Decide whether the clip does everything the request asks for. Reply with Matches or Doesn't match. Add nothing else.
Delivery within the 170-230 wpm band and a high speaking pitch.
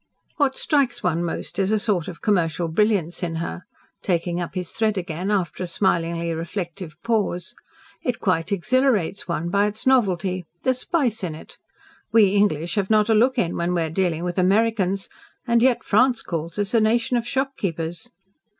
Matches